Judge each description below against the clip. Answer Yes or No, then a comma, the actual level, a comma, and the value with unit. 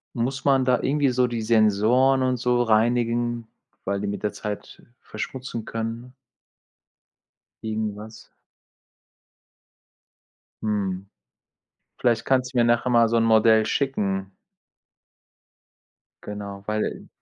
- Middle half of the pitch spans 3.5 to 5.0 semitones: No, average, 2.7 semitones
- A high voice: No, low, 115 Hz